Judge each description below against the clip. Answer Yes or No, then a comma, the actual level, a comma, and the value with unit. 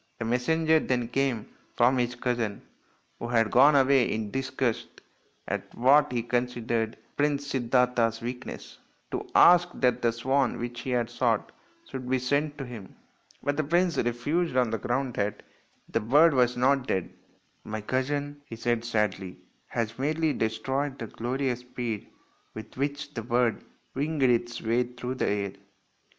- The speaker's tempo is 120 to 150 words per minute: No, average, 160 wpm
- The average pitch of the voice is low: Yes, low, 125 Hz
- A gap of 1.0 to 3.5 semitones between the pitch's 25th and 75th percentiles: Yes, average, 2.8 semitones